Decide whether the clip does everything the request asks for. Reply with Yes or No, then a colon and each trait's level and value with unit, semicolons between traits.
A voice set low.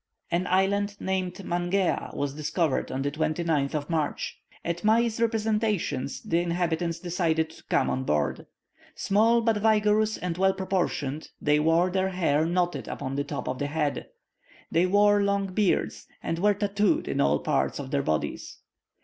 No: medium, 175 Hz